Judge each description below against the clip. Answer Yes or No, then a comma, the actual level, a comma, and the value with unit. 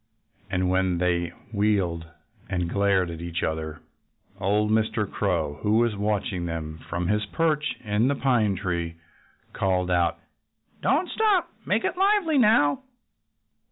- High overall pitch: No, low, 100 Hz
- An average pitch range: Yes, average, 4.5 semitones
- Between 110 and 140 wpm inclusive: Yes, slow, 135 wpm